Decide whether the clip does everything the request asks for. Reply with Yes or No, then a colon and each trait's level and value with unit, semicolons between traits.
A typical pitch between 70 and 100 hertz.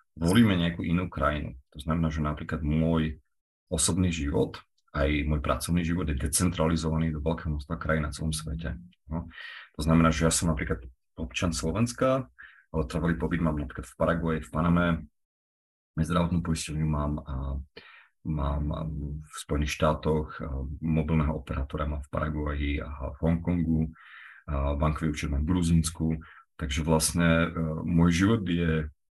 Yes: very low, 80 Hz